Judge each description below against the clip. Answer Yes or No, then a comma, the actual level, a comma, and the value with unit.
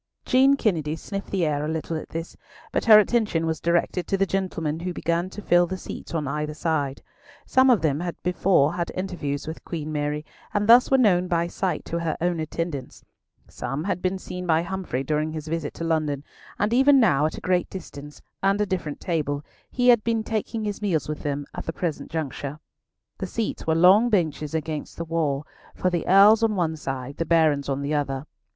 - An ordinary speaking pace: No, fast, 210 wpm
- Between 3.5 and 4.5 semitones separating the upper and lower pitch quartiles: Yes, average, 4.1 semitones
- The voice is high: No, medium, 165 Hz